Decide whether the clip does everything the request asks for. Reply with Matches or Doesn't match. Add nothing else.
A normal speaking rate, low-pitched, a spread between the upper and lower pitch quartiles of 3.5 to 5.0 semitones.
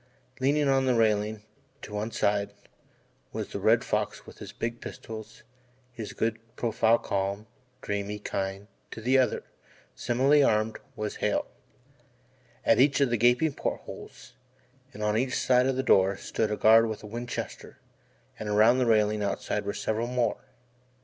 Doesn't match